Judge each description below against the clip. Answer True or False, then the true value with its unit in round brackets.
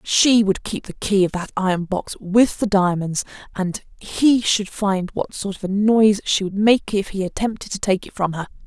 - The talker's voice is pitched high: True (200 Hz)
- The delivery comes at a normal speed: False (230 wpm)